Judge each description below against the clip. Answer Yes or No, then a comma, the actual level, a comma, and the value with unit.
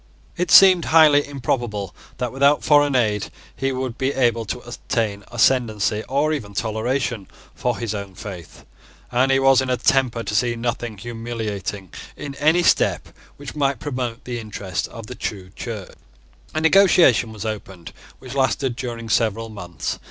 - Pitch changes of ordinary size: Yes, average, 3.9 semitones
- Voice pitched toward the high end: No, low, 120 Hz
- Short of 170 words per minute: Yes, average, 160 wpm